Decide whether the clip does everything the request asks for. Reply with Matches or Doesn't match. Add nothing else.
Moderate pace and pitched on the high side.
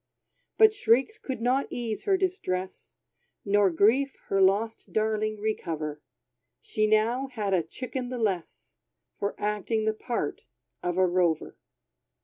Doesn't match